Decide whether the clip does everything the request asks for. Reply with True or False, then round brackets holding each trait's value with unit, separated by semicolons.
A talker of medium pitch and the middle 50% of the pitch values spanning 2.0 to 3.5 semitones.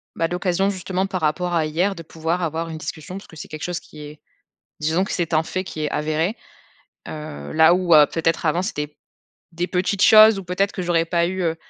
True (170 Hz; 2.6 semitones)